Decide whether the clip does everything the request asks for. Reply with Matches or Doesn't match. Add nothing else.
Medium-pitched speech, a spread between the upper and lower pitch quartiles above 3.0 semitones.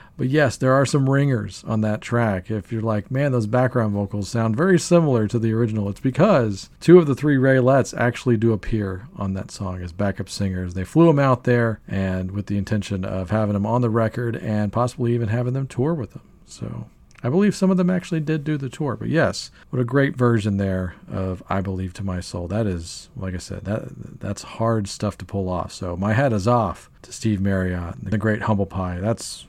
Doesn't match